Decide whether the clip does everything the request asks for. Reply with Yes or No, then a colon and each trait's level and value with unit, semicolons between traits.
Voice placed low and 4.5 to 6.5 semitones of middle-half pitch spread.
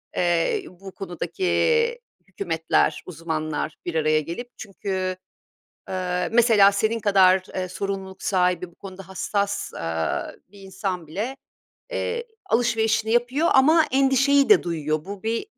No: high, 195 Hz; average, 4.8 semitones